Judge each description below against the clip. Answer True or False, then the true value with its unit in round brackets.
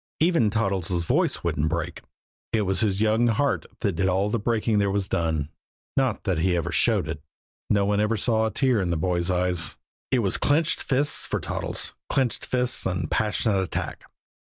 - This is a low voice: True (100 Hz)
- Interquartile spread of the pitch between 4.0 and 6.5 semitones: True (4.3 semitones)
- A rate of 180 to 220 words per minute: True (185 wpm)